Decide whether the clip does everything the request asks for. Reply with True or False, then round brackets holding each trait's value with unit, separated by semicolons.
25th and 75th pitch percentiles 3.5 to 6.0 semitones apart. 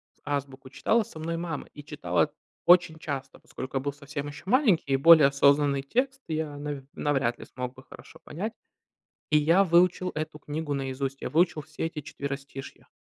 False (3.0 semitones)